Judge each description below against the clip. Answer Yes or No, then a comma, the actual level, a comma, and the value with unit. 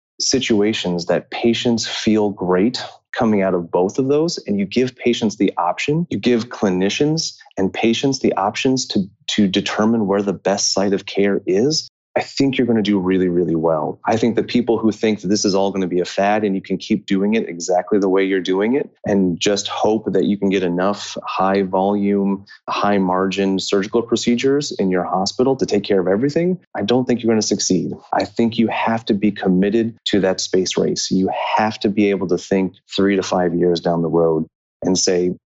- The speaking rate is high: Yes, fast, 215 wpm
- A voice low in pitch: Yes, low, 100 Hz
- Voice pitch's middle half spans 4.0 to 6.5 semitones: No, average, 3.5 semitones